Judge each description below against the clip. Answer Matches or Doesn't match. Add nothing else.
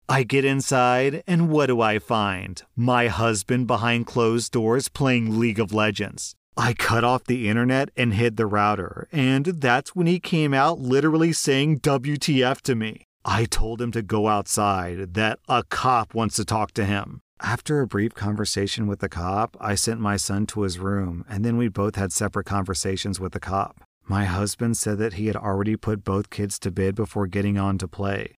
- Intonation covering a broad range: Doesn't match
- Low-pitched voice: Matches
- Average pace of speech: Matches